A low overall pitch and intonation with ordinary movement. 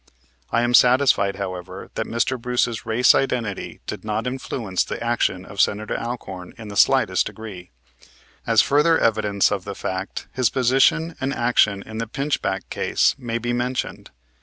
Yes: low, 115 Hz; average, 3.9 semitones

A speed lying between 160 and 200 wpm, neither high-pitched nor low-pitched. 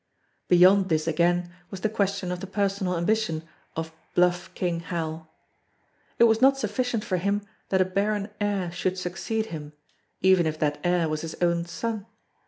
Yes: average, 170 wpm; medium, 180 Hz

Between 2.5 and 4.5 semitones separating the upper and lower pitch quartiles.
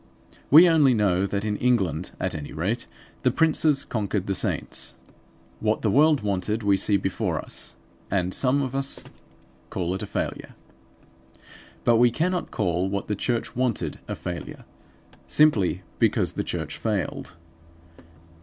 No: average, 5.2 semitones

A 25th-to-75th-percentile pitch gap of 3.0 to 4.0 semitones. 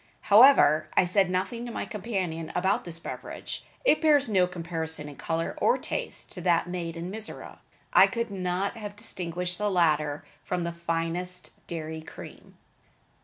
Yes: average, 3.4 semitones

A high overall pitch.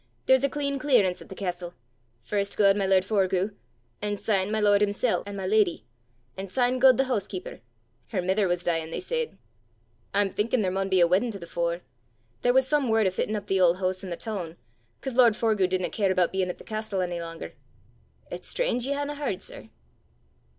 Yes: high, 200 Hz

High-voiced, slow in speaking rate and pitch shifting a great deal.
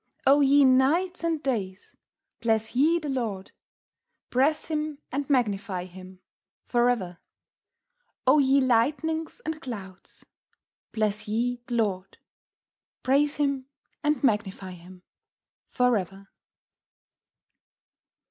Yes: high, 245 Hz; slow, 105 wpm; wide, 6.3 semitones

